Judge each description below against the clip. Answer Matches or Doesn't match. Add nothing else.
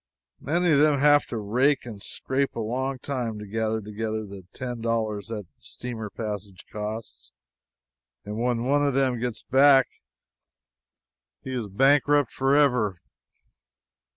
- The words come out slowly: Doesn't match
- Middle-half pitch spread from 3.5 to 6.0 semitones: Matches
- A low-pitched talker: Matches